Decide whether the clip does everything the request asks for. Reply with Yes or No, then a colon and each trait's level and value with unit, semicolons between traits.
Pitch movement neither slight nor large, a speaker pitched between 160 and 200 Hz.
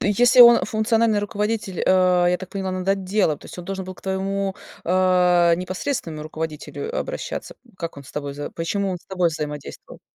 Yes: average, 3.0 semitones; medium, 185 Hz